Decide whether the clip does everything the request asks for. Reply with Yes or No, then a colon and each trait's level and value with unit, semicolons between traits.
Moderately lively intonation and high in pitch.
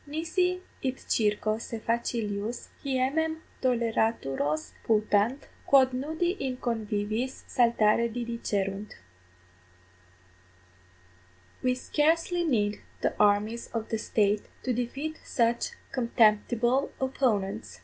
Yes: average, 3.9 semitones; high, 235 Hz